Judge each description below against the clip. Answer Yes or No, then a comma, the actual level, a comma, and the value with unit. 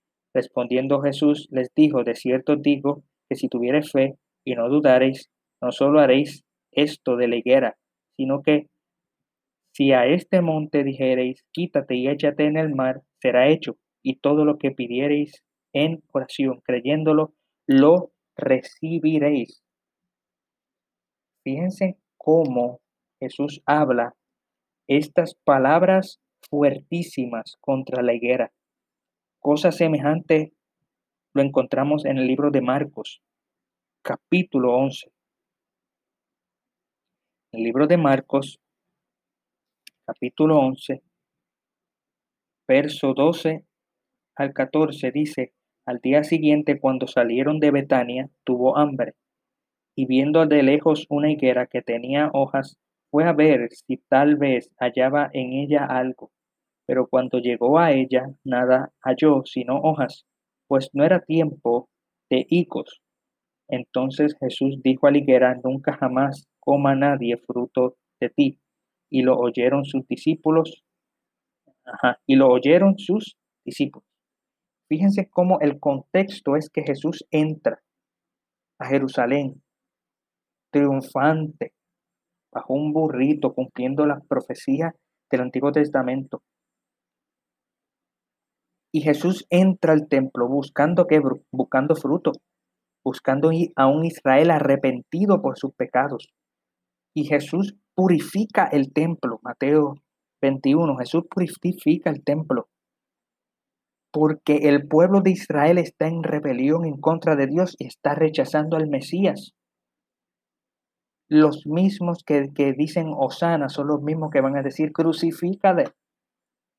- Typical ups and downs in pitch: Yes, average, 3.1 semitones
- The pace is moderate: No, slow, 115 wpm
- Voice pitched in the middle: Yes, medium, 145 Hz